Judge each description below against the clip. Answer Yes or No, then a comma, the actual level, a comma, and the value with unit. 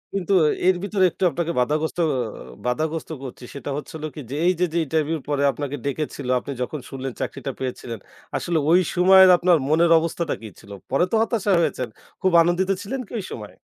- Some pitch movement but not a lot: Yes, average, 4.4 semitones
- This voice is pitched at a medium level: Yes, medium, 160 Hz